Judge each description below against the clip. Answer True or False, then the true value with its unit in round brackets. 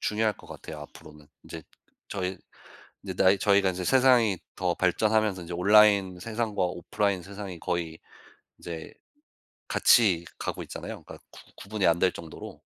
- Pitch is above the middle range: False (95 Hz)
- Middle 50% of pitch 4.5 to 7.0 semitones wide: False (3.5 semitones)